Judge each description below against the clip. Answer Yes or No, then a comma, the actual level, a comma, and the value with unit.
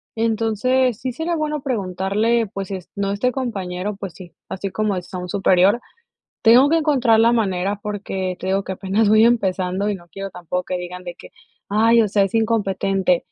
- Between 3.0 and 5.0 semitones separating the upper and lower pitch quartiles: Yes, average, 3.5 semitones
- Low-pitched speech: No, high, 200 Hz